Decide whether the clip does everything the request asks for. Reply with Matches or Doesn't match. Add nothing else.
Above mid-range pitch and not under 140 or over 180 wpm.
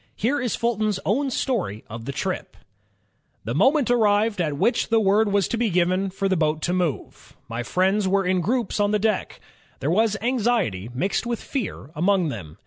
Doesn't match